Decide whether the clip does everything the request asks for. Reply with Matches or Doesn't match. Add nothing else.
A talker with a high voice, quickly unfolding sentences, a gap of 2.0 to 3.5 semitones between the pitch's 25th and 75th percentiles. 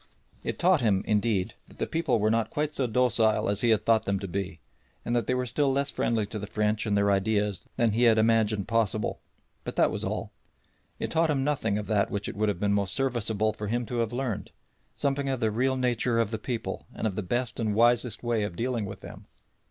Doesn't match